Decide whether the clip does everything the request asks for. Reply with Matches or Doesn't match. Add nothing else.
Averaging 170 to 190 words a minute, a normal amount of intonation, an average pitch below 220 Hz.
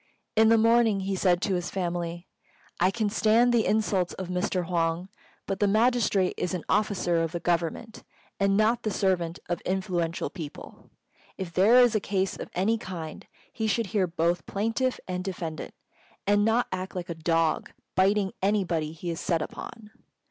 Matches